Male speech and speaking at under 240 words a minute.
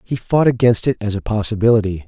Yes: male; fast, 205 wpm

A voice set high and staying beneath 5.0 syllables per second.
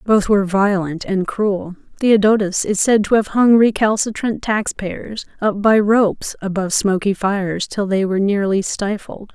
Yes: high, 200 Hz; 4.6 syllables/s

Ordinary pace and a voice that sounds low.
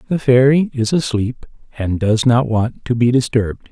Yes: average, 180 wpm; low, 120 Hz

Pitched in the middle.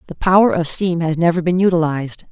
Yes: medium, 170 Hz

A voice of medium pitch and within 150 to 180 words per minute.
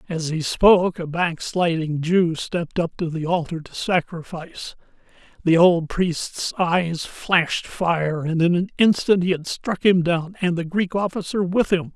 Yes: medium, 175 Hz; average, 170 wpm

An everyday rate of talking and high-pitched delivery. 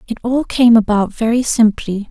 Yes: average, 170 wpm; high, 230 Hz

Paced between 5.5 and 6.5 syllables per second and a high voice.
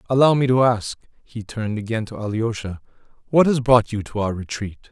No: 5.7 syllables/s; low, 115 Hz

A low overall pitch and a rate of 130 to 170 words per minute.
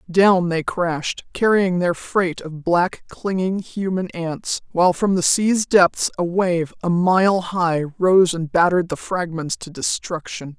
No: medium, 175 Hz; average, 160 wpm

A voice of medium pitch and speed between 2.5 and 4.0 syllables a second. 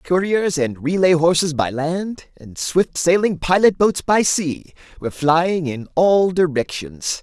Yes: medium, 165 Hz; 3.9 syllables/s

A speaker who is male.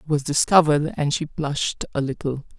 No: female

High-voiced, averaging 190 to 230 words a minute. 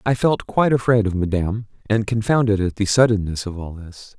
No: low, 105 Hz; average, 200 wpm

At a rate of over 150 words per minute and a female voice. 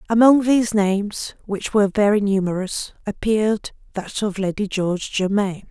No: slow, 135 wpm; female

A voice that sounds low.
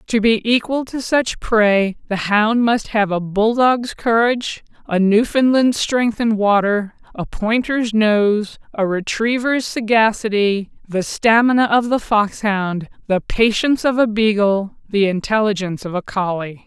No: high, 215 Hz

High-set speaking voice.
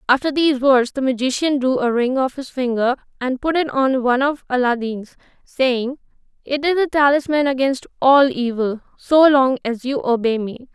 Yes: very high, 265 Hz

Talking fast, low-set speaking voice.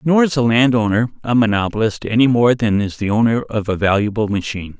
Yes: fast, 215 wpm; low, 115 Hz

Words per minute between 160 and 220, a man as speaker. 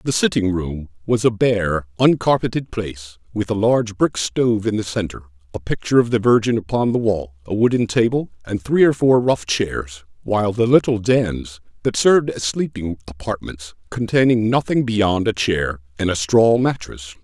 Yes: average, 180 wpm; male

